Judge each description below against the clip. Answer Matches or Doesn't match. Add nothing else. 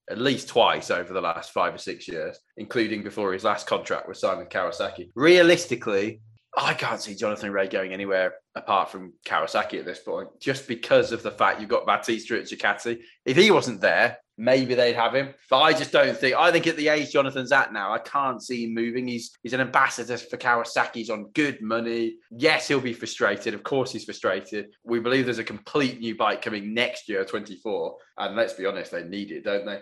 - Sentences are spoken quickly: Matches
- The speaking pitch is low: Matches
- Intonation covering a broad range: Matches